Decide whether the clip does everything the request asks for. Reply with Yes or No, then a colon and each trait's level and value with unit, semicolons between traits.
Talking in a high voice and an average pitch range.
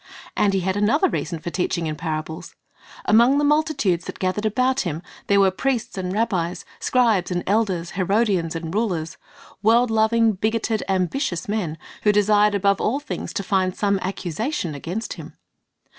Yes: high, 200 Hz; average, 4.0 semitones